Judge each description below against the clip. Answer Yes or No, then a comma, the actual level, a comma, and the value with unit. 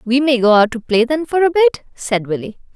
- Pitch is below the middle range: No, very high, 260 Hz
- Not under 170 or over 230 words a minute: No, fast, 260 wpm